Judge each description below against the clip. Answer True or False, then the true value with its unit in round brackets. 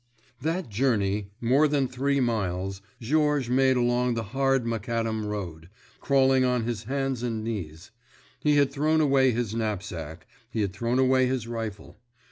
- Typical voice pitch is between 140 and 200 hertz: False (120 Hz)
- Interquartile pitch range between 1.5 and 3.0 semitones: False (4.2 semitones)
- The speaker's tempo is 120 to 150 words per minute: True (140 wpm)